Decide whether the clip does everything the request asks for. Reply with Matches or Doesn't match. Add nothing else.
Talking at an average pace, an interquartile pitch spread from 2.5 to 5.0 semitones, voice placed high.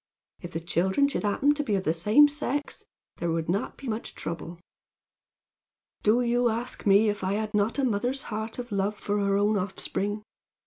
Matches